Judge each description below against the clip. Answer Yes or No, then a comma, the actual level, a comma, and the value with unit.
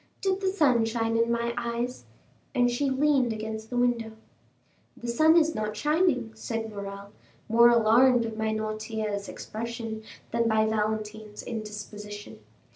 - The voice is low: No, high, 225 Hz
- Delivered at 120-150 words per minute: Yes, slow, 135 wpm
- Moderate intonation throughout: No, narrow, 2.1 semitones